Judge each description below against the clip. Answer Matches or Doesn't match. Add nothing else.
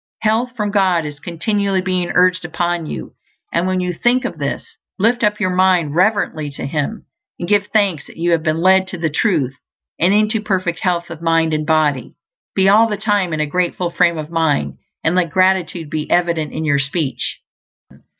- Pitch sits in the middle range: Matches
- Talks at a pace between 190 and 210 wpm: Matches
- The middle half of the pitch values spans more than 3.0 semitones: Matches